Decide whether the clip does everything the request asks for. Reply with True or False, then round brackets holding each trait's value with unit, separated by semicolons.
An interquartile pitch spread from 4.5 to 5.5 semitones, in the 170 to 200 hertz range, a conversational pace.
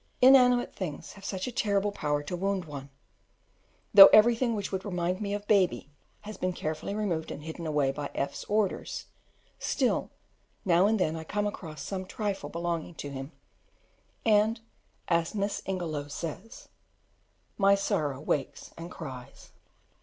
True (4.9 semitones; 185 Hz; 155 wpm)